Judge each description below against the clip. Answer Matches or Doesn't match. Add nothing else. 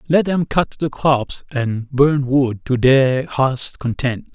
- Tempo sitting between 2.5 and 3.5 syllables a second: Matches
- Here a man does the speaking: Matches